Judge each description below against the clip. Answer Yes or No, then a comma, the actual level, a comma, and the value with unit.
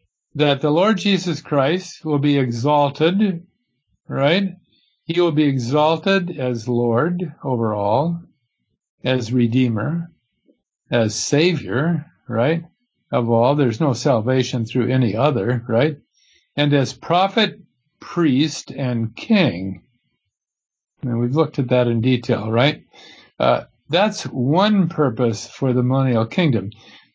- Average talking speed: No, slow, 115 wpm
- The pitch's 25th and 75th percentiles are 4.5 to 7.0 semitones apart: Yes, average, 5.2 semitones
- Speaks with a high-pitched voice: No, medium, 140 Hz